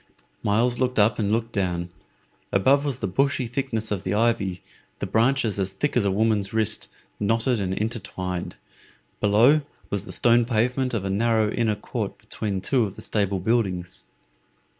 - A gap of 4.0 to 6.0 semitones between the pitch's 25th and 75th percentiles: No, average, 3.3 semitones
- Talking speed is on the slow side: No, average, 165 wpm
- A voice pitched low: Yes, low, 110 Hz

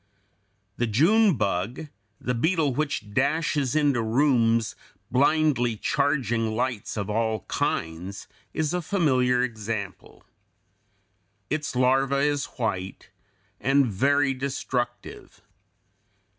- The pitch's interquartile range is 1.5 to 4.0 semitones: No, average, 4.5 semitones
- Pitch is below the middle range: Yes, low, 125 Hz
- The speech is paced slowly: Yes, slow, 100 wpm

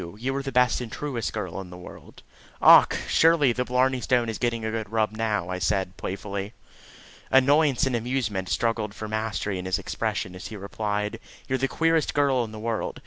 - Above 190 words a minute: Yes, average, 200 wpm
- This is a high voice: No, low, 115 Hz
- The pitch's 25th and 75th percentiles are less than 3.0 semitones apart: No, average, 3.7 semitones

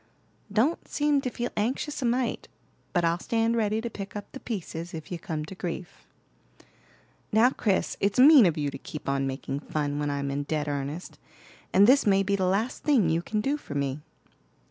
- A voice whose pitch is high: Yes, high, 195 Hz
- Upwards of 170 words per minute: Yes, average, 200 wpm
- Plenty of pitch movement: Yes, wide, 7.4 semitones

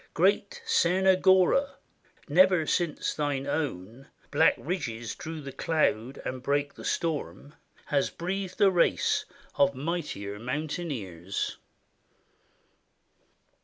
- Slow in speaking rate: Yes, slow, 95 wpm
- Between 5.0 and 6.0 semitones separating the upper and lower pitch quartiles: Yes, wide, 5.5 semitones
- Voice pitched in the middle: Yes, medium, 150 Hz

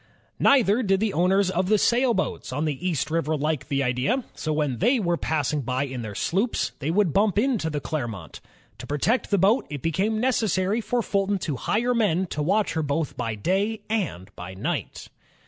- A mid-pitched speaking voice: Yes, medium, 180 Hz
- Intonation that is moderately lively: No, wide, 6.5 semitones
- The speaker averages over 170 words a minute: Yes, average, 200 wpm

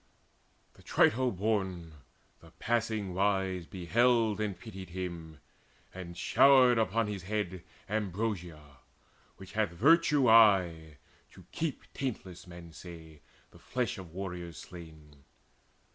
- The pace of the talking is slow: Yes, slow, 115 wpm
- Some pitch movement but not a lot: Yes, average, 4.4 semitones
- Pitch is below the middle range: Yes, very low, 95 Hz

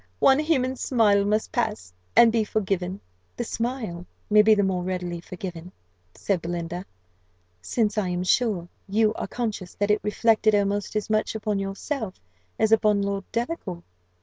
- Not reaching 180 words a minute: Yes, average, 155 wpm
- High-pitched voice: Yes, high, 205 Hz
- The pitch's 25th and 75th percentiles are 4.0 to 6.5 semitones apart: No, average, 3.2 semitones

